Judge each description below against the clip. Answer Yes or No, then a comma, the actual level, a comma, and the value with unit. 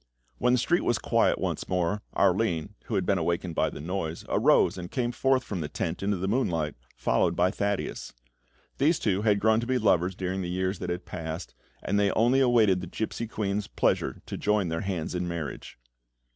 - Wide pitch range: No, average, 4.0 semitones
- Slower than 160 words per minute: No, average, 200 wpm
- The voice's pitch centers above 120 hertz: No, very low, 95 Hz